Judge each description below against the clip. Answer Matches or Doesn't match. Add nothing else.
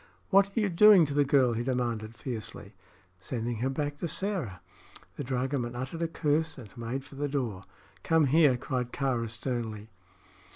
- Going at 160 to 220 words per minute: Matches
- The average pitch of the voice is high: Doesn't match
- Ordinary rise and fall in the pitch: Matches